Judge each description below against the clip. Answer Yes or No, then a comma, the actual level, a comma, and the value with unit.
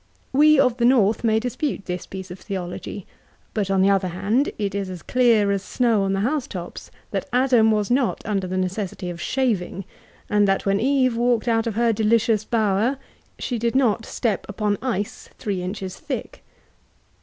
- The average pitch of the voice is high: Yes, high, 215 Hz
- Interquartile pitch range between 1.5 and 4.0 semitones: Yes, average, 3.7 semitones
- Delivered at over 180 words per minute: Yes, average, 190 wpm